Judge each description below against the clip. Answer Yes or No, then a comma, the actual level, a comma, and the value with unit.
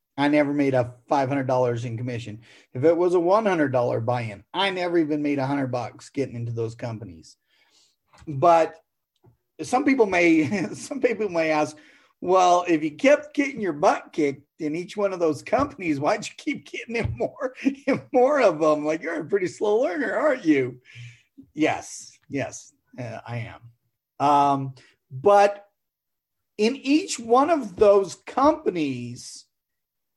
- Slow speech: No, average, 150 wpm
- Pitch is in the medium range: Yes, medium, 160 Hz